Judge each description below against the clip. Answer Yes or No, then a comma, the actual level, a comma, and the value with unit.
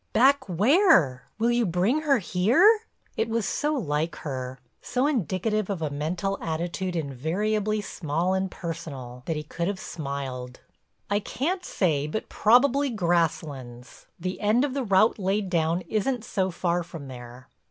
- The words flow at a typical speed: Yes, average, 150 wpm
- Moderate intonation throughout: No, wide, 6.2 semitones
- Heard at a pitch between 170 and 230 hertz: Yes, medium, 185 Hz